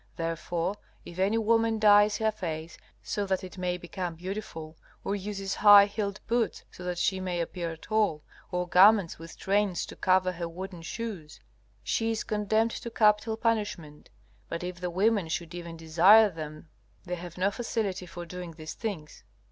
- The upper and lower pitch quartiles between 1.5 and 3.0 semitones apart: No, average, 3.6 semitones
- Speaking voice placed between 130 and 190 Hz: Yes, medium, 185 Hz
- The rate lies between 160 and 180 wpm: Yes, average, 170 wpm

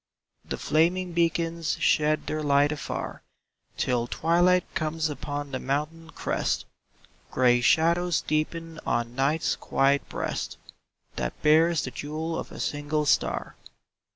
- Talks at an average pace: No, slow, 125 wpm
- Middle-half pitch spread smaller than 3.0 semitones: Yes, narrow, 2.5 semitones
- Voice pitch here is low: No, medium, 155 Hz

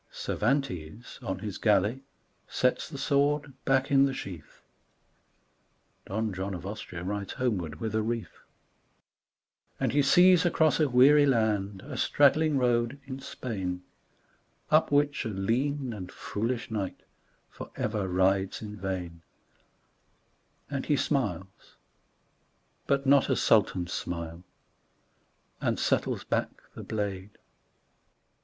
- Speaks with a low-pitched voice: Yes, low, 110 Hz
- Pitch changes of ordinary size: No, wide, 6.1 semitones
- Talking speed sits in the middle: No, slow, 120 wpm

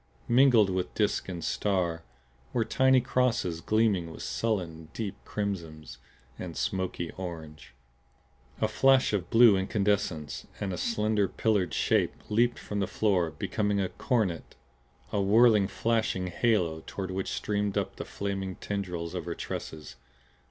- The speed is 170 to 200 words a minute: No, average, 140 wpm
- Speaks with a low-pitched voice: Yes, low, 100 Hz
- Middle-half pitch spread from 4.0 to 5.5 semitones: No, average, 3.6 semitones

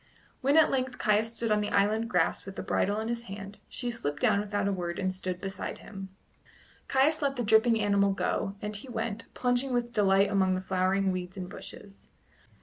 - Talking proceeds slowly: No, fast, 205 wpm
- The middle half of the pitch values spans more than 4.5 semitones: No, average, 3.4 semitones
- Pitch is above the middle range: Yes, high, 205 Hz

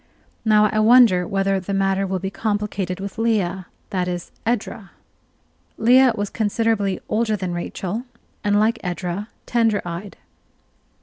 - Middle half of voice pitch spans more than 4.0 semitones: No, average, 2.7 semitones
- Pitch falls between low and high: No, high, 200 Hz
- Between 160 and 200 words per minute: No, slow, 135 wpm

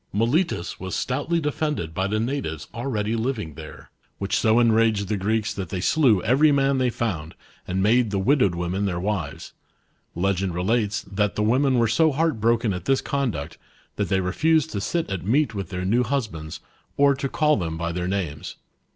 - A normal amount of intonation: No, wide, 6.0 semitones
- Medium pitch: No, low, 110 Hz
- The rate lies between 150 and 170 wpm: No, average, 190 wpm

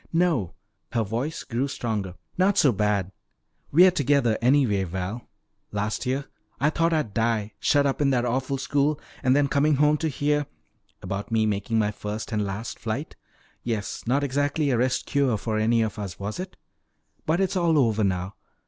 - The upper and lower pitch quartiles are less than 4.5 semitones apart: No, average, 5.2 semitones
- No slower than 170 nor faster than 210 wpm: Yes, average, 180 wpm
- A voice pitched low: Yes, low, 125 Hz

